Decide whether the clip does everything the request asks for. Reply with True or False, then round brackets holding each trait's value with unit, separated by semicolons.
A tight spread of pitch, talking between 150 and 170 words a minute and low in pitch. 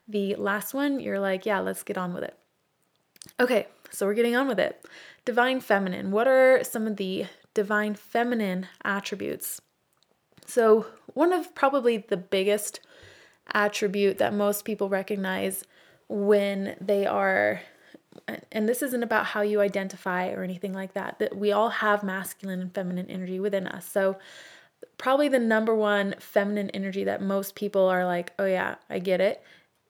False (2.3 semitones; 160 wpm; 205 Hz)